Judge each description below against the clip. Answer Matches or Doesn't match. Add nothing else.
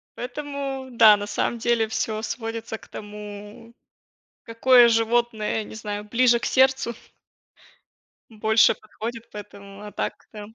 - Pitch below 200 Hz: Doesn't match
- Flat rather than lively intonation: Matches